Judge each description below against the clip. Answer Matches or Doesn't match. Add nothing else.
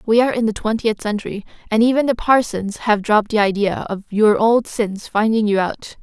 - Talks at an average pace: Doesn't match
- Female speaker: Matches